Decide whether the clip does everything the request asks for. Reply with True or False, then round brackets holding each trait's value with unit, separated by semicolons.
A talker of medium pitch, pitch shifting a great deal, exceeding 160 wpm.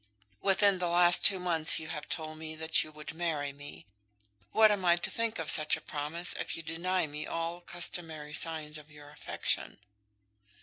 False (160 Hz; 2.5 semitones; 185 wpm)